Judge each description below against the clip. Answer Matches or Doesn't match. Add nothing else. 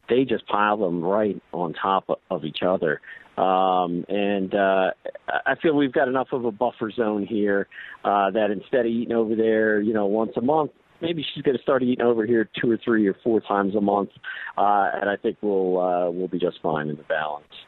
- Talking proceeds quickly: Matches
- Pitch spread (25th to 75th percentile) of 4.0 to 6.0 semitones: Doesn't match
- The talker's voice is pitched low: Matches